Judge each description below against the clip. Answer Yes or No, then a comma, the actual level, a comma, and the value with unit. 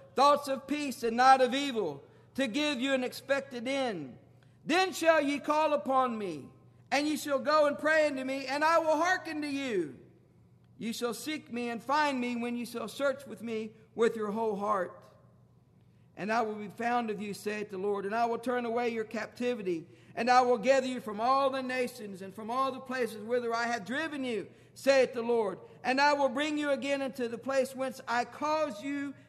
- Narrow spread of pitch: No, average, 3.3 semitones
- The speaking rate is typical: No, fast, 210 wpm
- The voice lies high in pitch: Yes, very high, 255 Hz